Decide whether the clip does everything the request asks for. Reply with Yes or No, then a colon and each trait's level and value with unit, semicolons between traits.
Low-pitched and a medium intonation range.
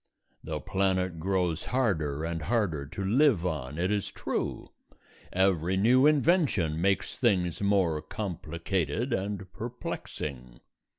Yes: very low, 95 Hz; average, 4.4 semitones